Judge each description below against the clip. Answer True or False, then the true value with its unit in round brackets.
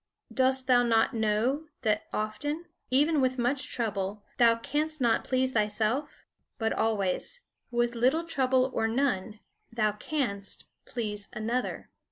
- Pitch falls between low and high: False (240 Hz)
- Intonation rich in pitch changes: False (3.6 semitones)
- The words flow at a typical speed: False (130 wpm)